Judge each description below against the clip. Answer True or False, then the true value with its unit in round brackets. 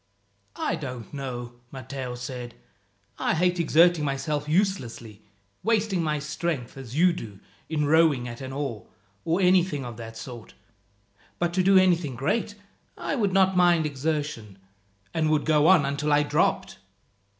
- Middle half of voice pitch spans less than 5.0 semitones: False (5.4 semitones)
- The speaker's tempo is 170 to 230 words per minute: False (150 wpm)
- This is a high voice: False (150 Hz)